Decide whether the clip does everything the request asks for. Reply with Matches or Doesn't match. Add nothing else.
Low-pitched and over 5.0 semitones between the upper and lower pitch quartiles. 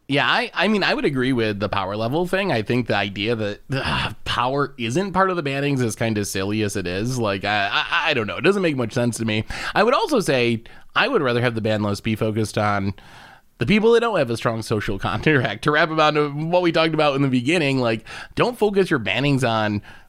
Matches